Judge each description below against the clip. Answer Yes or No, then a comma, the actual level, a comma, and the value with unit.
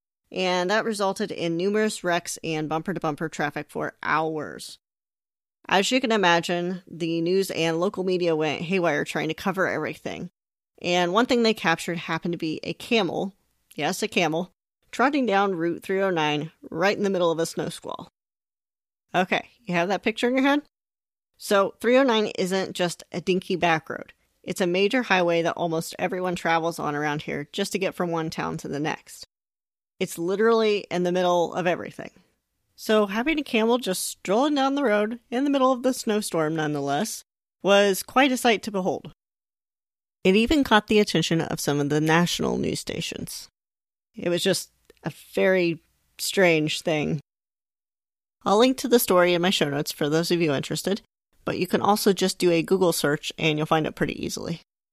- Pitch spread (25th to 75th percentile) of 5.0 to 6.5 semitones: No, average, 4.2 semitones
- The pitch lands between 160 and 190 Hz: Yes, medium, 185 Hz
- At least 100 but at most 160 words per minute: No, average, 180 wpm